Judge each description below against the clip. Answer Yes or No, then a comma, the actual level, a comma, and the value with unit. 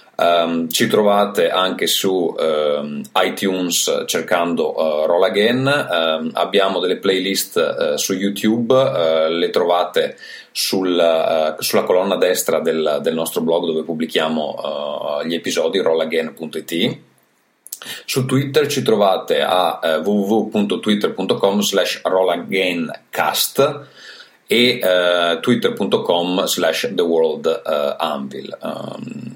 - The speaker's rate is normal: No, slow, 100 wpm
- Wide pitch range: Yes, wide, 7.8 semitones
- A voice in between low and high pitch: No, very low, 95 Hz